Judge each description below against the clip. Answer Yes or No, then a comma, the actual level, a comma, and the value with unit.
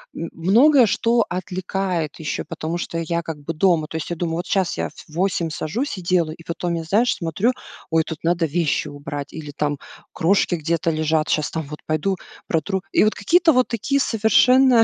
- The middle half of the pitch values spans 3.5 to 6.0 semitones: Yes, average, 3.8 semitones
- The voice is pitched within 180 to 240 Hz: No, medium, 170 Hz